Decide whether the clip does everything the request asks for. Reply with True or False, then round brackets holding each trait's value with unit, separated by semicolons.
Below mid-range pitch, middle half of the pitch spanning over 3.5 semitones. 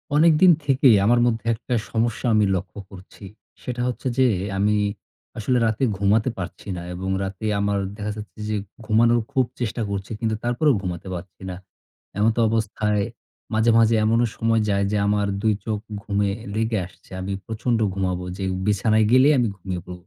False (110 Hz; 2.8 semitones)